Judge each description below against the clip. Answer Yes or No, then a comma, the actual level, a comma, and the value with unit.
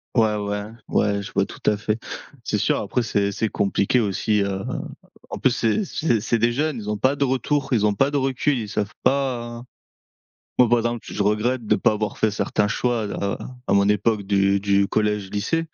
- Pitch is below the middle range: Yes, low, 110 Hz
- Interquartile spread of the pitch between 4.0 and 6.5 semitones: No, average, 3.3 semitones